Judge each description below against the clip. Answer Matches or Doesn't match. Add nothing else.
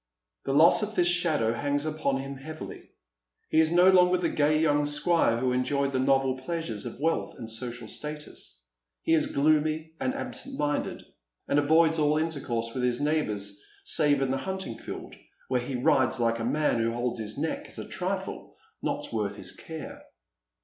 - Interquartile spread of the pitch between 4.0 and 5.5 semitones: Matches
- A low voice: Doesn't match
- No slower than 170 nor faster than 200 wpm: Matches